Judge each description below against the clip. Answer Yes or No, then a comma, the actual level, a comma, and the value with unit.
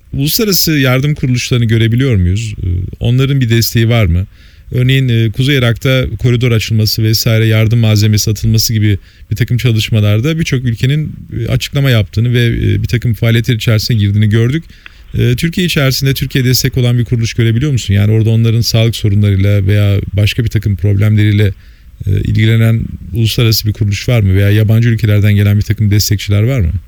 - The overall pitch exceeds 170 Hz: No, low, 115 Hz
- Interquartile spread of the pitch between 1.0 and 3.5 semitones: Yes, average, 3.0 semitones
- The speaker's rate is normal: No, fast, 150 wpm